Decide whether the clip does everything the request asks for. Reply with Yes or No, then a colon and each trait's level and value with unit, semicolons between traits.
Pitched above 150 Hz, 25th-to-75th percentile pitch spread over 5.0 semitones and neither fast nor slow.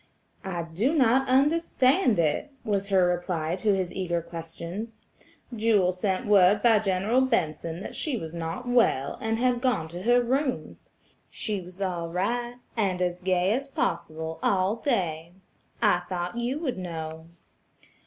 Yes: high, 190 Hz; wide, 5.6 semitones; average, 150 wpm